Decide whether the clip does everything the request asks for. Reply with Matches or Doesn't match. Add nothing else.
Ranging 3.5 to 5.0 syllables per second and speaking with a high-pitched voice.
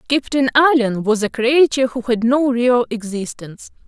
Matches